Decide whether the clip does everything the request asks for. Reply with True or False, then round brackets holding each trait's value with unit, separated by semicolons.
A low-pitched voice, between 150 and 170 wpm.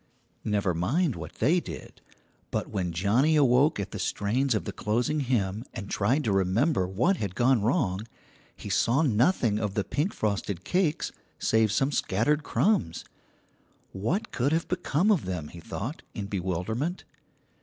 True (110 Hz; 155 wpm)